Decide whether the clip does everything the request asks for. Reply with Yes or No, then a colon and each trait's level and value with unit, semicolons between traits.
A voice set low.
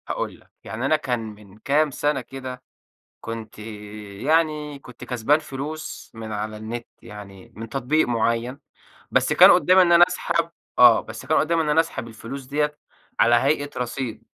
Yes: low, 130 Hz